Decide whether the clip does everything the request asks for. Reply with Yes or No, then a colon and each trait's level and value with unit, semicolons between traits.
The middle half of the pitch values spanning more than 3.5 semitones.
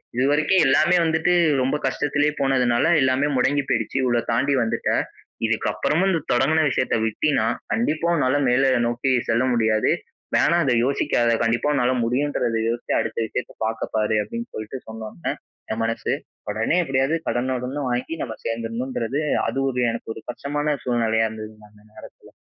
Yes: average, 4.0 semitones